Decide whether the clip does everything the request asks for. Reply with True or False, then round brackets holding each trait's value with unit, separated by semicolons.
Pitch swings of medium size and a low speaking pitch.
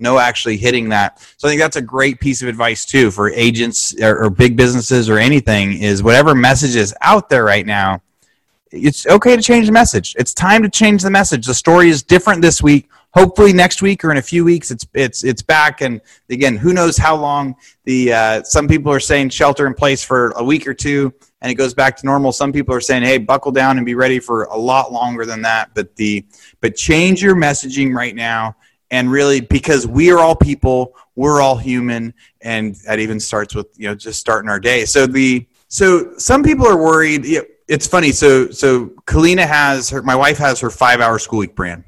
True (4.2 semitones; 130 Hz)